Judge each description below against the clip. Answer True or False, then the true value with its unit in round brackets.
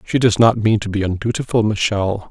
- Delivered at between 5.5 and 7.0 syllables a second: True (5.6 syllables/s)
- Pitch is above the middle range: False (110 Hz)